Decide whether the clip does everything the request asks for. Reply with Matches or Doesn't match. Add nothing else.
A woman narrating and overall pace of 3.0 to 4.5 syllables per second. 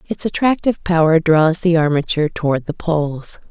Doesn't match